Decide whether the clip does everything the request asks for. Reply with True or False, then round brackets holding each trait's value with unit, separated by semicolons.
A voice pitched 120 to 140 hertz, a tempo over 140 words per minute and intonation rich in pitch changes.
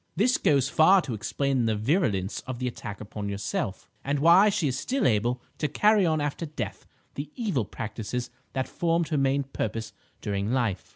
True (135 Hz; 180 wpm; 6.2 semitones)